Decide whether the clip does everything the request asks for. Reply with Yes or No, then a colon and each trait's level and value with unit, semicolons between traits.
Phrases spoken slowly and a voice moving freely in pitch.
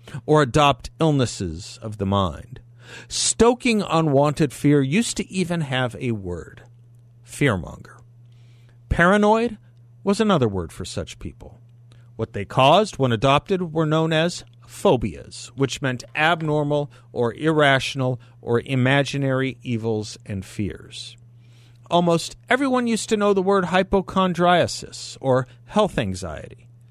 No: slow, 120 wpm; average, 5.0 semitones